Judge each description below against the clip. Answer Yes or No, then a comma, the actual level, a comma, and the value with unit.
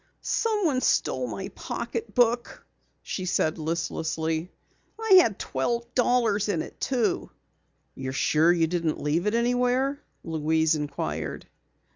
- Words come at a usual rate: No, slow, 115 wpm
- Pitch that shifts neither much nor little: No, wide, 7.6 semitones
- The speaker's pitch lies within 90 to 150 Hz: No, medium, 185 Hz